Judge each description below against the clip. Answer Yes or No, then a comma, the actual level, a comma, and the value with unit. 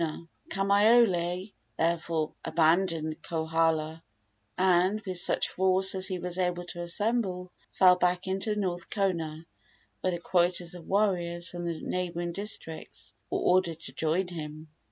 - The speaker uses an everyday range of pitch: No, narrow, 2.1 semitones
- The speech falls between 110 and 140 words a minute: Yes, slow, 135 wpm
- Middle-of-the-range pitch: Yes, medium, 180 Hz